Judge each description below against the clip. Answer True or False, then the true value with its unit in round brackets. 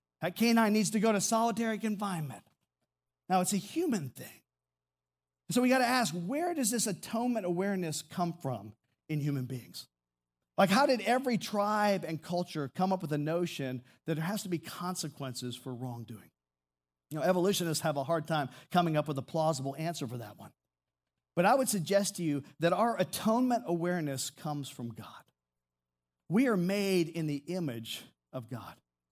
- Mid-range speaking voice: True (160 Hz)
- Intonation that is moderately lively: False (8.2 semitones)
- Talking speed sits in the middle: True (175 wpm)